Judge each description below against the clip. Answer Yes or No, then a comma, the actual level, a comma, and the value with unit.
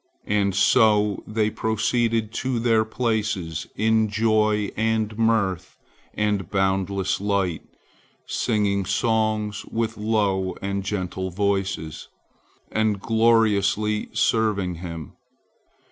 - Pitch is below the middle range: Yes, low, 105 Hz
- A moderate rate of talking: No, slow, 95 wpm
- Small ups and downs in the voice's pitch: Yes, narrow, 2.2 semitones